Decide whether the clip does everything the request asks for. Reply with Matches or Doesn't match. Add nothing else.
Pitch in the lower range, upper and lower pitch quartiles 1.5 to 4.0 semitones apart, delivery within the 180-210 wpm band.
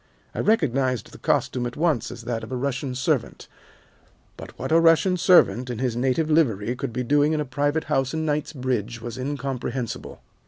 Matches